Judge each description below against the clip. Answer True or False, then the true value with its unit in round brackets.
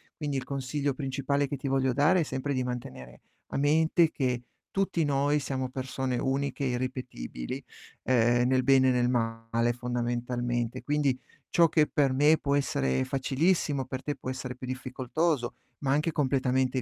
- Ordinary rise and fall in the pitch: False (2.2 semitones)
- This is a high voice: False (130 Hz)